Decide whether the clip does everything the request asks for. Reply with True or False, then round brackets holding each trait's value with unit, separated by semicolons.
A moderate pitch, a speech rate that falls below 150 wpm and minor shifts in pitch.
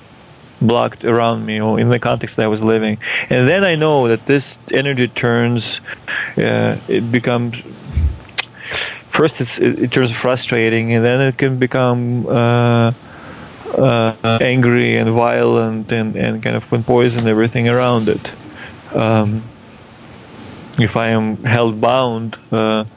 False (115 Hz; 140 wpm; 1.6 semitones)